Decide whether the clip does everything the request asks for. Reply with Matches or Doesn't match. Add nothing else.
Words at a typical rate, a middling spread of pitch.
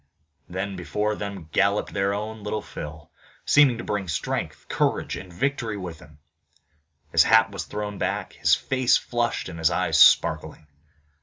Matches